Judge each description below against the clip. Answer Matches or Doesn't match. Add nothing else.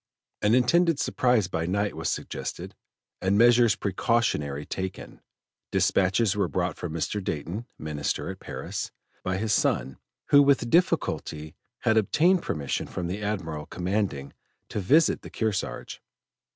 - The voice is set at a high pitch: Doesn't match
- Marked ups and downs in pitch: Matches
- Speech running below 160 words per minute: Matches